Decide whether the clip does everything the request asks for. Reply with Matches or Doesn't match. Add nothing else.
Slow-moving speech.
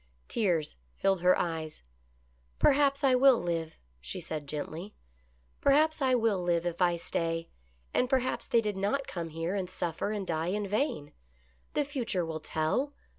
Doesn't match